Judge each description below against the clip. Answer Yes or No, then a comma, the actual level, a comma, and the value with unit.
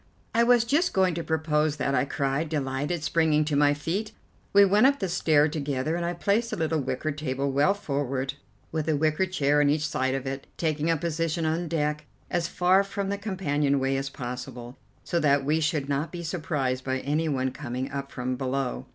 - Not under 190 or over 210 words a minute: Yes, fast, 205 wpm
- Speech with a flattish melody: No, average, 3.7 semitones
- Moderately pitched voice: Yes, medium, 150 Hz